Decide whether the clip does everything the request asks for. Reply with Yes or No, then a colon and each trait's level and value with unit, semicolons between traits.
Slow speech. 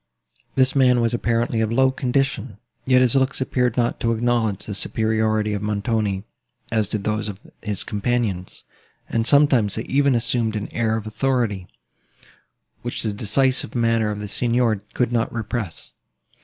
No: average, 155 wpm